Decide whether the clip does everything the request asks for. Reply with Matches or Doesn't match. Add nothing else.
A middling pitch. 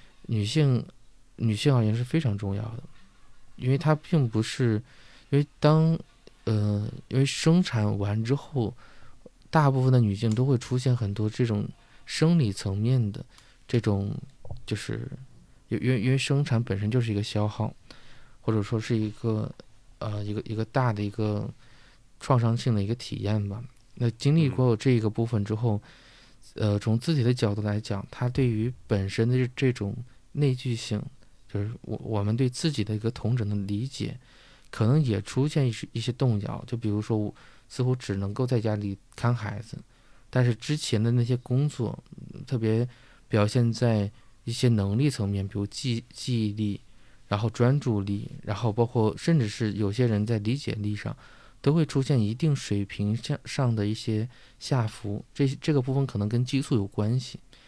Doesn't match